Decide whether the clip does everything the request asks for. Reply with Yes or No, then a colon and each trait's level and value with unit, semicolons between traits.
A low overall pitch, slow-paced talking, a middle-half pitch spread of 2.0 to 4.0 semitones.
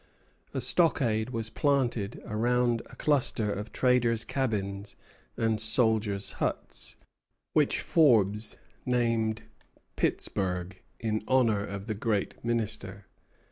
Yes: low, 110 Hz; slow, 100 wpm; average, 3.0 semitones